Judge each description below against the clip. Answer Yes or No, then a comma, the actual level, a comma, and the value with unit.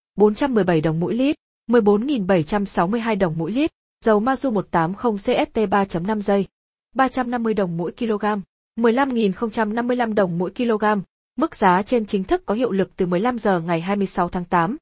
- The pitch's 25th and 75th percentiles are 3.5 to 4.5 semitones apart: Yes, average, 4.2 semitones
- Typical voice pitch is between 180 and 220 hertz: Yes, high, 210 Hz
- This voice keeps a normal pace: No, slow, 145 wpm